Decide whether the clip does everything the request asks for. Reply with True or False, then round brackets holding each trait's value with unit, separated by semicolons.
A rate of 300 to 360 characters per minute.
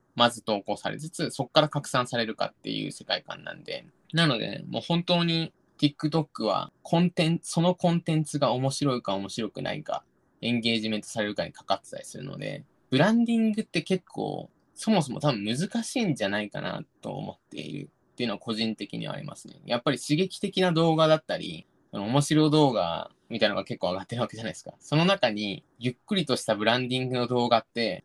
False (440 characters per minute)